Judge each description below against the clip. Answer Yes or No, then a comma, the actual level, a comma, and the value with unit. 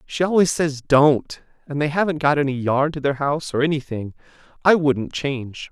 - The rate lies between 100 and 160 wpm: No, average, 190 wpm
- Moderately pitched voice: Yes, medium, 145 Hz